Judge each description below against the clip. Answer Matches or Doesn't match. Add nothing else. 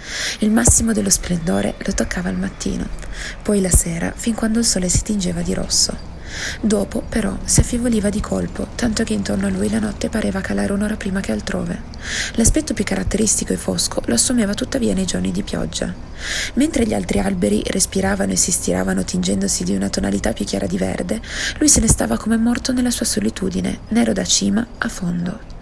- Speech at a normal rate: Doesn't match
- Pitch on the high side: Matches